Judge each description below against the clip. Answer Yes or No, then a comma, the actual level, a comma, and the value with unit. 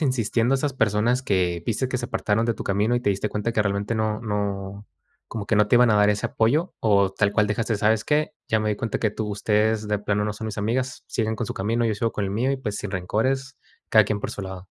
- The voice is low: Yes, low, 110 Hz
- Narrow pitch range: Yes, narrow, 2.3 semitones